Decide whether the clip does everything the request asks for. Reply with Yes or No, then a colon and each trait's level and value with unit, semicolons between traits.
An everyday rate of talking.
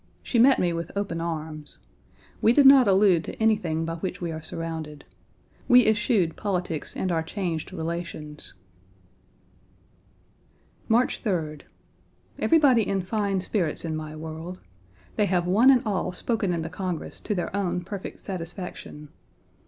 Yes: average, 145 wpm